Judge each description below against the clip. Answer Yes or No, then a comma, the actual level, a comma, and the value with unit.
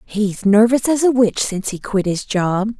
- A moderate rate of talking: No, fast, 215 wpm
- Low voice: No, high, 215 Hz